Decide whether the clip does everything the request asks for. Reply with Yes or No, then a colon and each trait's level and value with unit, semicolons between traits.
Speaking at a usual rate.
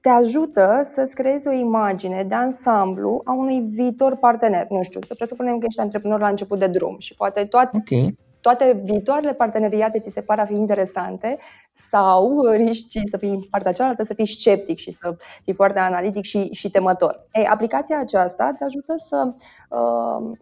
No: fast, 175 wpm